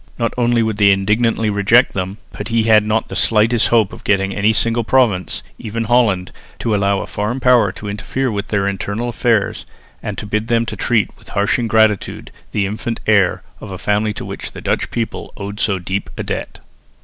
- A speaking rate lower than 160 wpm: No, average, 200 wpm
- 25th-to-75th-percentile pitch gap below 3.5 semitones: Yes, narrow, 2.4 semitones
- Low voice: Yes, low, 105 Hz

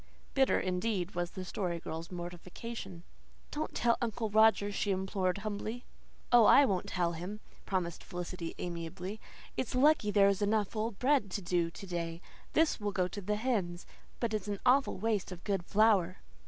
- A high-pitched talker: Yes, high, 200 Hz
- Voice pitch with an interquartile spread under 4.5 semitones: Yes, average, 3.7 semitones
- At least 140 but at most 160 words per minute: No, average, 170 wpm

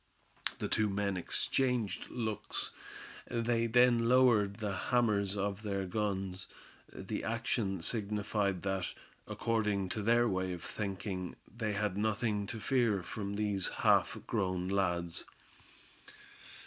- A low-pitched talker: Yes, low, 105 Hz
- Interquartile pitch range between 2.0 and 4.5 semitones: Yes, average, 2.8 semitones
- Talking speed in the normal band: No, slow, 120 wpm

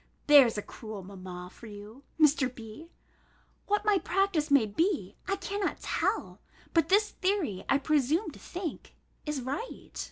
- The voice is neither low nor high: No, very high, 290 Hz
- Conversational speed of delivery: Yes, average, 150 wpm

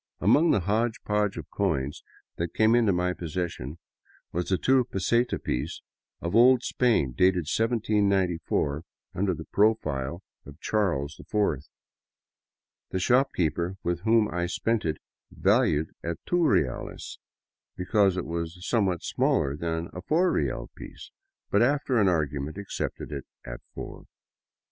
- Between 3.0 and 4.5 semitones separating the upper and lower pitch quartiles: No, average, 5.1 semitones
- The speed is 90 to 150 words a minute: Yes, slow, 135 wpm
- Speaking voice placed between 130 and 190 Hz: No, very low, 90 Hz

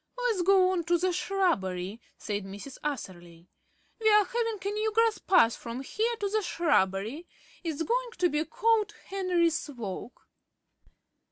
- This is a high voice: Yes, very high, 345 Hz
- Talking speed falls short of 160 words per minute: Yes, average, 150 wpm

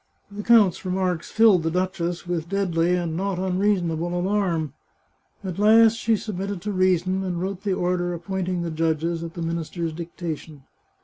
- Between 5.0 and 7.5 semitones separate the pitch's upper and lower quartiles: No, narrow, 2.5 semitones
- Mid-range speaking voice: Yes, medium, 180 Hz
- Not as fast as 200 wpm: Yes, average, 160 wpm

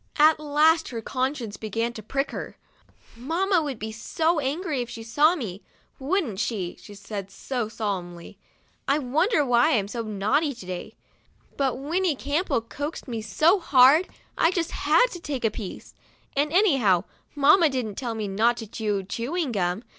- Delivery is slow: No, average, 175 wpm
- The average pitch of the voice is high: Yes, very high, 255 Hz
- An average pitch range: No, wide, 6.0 semitones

